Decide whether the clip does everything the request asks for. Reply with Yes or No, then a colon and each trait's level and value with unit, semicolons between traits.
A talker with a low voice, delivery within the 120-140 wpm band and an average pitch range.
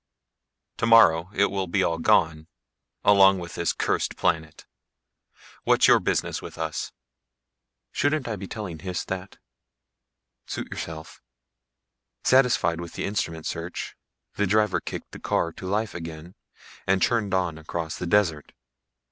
Yes: very low, 90 Hz; slow, 135 wpm; average, 3.7 semitones